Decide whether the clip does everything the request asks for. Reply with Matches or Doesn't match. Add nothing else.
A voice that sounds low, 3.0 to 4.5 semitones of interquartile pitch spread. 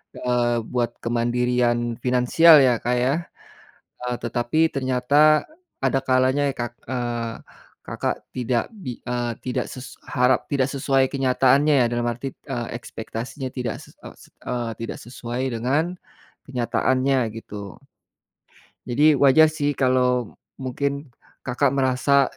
Doesn't match